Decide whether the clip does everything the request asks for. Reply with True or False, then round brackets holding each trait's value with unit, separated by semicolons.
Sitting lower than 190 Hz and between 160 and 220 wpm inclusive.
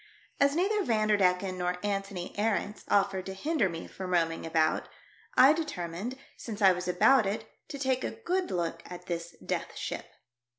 False (195 Hz; 165 wpm)